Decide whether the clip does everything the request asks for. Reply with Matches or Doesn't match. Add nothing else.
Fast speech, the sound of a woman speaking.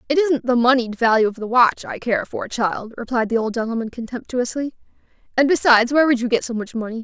Matches